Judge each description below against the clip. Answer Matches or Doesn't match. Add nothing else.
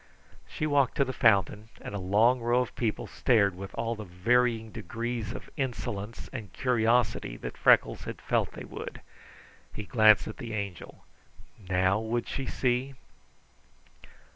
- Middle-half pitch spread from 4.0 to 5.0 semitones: Doesn't match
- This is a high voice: Doesn't match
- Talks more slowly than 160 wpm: Matches